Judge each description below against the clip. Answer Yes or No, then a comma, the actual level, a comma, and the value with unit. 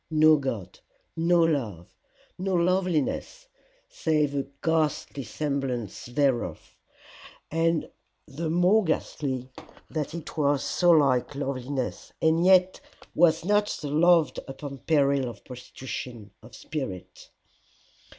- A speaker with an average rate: No, slow, 110 wpm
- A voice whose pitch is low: No, medium, 150 Hz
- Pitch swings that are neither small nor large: Yes, average, 3.9 semitones